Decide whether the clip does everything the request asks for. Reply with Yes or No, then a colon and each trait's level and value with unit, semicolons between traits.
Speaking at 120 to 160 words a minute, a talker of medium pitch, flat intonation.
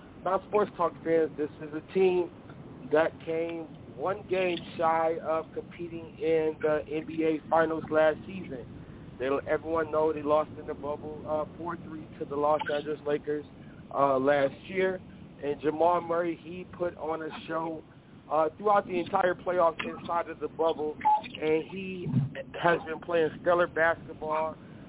Yes: average, 150 wpm; medium, 160 Hz; narrow, 2.1 semitones